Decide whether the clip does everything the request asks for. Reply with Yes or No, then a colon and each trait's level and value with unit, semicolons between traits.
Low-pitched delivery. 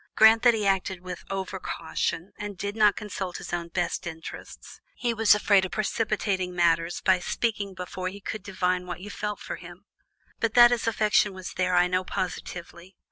No: high, 190 Hz